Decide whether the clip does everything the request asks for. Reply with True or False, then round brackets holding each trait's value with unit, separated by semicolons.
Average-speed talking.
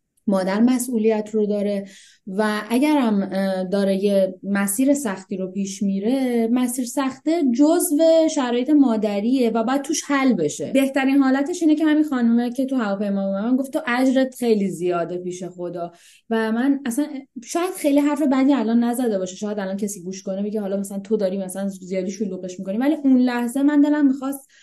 True (175 wpm)